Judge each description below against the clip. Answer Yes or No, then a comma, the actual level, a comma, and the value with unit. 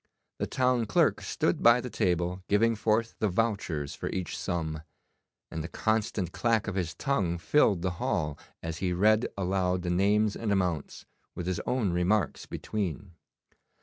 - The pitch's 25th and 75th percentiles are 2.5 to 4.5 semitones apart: Yes, average, 3.8 semitones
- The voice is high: No, very low, 95 Hz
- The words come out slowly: No, average, 160 wpm